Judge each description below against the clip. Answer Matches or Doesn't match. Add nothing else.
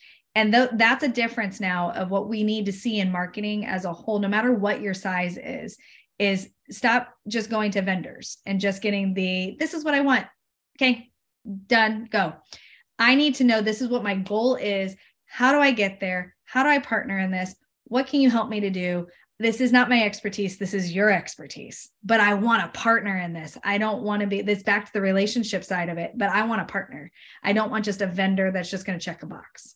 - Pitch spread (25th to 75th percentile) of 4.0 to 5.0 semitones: Doesn't match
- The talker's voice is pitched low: Doesn't match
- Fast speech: Matches